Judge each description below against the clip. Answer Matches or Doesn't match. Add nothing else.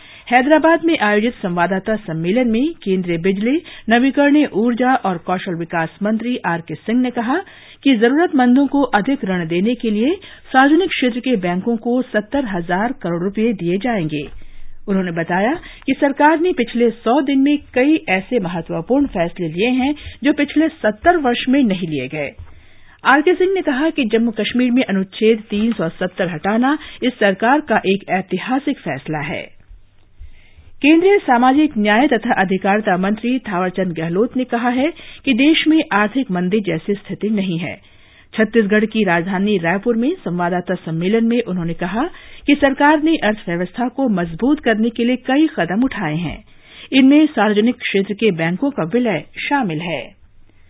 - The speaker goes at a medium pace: Matches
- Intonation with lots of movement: Matches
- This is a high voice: Matches